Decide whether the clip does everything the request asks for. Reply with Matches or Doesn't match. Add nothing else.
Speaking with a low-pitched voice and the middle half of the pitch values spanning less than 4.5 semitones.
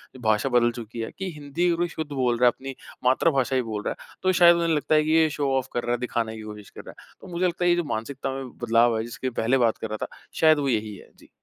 Doesn't match